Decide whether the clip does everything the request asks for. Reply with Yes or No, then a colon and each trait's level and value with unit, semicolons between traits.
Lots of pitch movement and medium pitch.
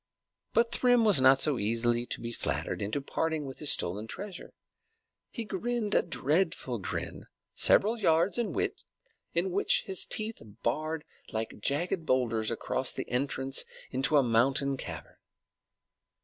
Yes: wide, 7.6 semitones; medium, 145 Hz